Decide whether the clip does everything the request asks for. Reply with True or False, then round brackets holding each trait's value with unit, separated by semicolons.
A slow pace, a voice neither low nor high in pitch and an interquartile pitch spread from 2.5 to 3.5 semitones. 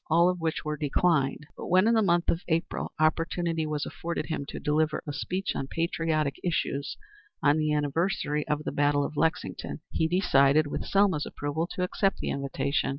False (185 wpm; 155 Hz; 2.8 semitones)